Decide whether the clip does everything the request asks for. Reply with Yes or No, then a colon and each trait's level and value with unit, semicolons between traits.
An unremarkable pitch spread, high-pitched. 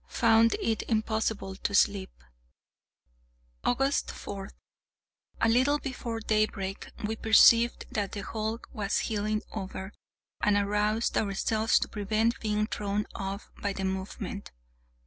No: narrow, 1.9 semitones; high, 215 Hz